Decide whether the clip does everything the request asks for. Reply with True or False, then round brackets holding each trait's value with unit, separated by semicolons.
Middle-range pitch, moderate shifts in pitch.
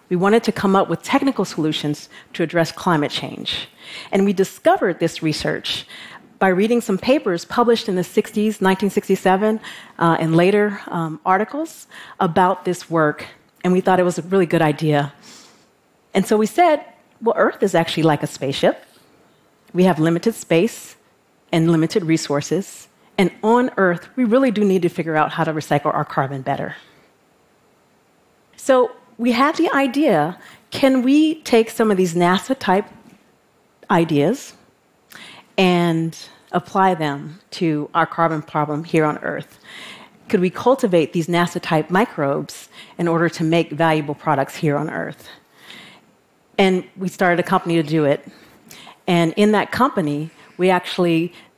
True (180 Hz; 4.5 semitones)